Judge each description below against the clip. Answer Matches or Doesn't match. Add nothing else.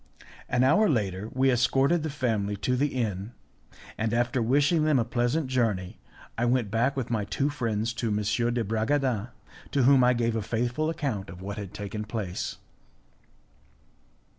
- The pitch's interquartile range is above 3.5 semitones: Matches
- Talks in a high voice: Doesn't match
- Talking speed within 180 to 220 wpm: Doesn't match